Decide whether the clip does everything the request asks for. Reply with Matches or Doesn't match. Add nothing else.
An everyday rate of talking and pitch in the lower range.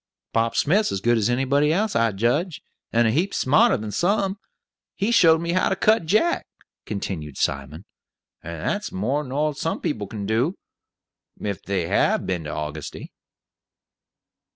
Matches